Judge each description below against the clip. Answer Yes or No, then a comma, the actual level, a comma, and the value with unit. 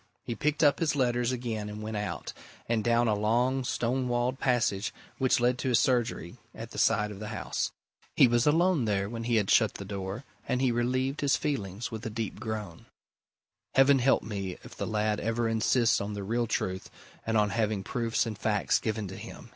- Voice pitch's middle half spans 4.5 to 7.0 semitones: No, average, 3.0 semitones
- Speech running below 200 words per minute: No, fast, 205 wpm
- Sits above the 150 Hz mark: No, low, 115 Hz